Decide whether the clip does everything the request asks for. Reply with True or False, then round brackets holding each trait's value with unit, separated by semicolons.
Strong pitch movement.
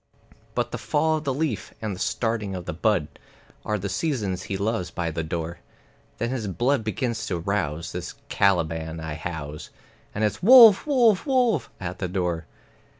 True (7.2 semitones)